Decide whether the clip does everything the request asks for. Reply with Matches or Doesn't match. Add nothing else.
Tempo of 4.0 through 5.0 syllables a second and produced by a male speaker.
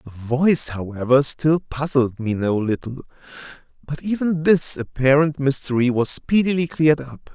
Matches